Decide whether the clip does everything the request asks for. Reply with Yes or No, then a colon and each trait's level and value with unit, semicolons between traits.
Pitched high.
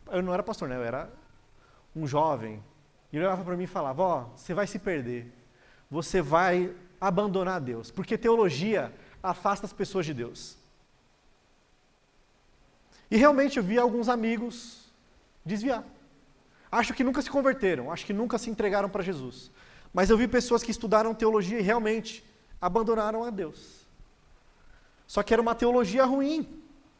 Yes: high, 205 Hz